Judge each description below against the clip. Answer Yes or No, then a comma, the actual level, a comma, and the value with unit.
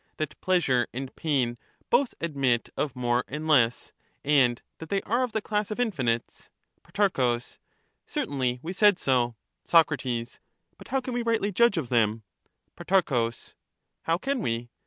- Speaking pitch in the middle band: Yes, medium, 145 Hz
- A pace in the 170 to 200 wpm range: No, average, 150 wpm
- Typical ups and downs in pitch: No, wide, 8.6 semitones